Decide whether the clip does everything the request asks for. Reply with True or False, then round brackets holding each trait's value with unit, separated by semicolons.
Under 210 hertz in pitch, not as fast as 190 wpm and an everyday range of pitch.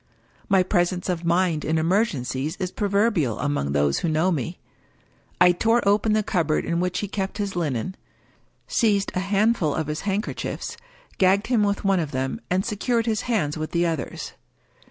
True (185 Hz; 180 wpm; 4.5 semitones)